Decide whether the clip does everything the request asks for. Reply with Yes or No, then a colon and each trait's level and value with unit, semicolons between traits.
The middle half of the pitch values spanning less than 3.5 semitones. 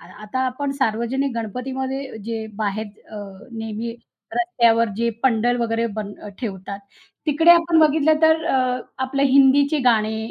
No: average, 4.0 semitones